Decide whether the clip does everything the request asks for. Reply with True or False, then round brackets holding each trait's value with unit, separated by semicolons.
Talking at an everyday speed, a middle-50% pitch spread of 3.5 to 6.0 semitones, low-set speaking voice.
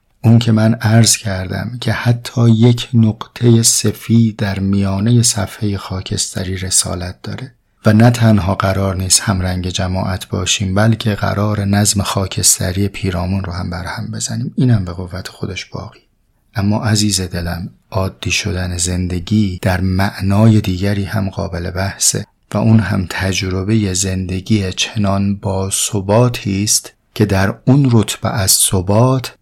False (135 wpm; 2.8 semitones; 100 Hz)